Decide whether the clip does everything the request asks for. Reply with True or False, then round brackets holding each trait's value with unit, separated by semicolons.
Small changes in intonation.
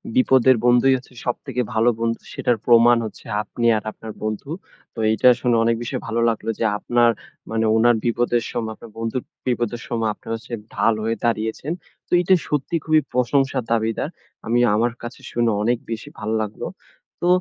True (1.6 semitones)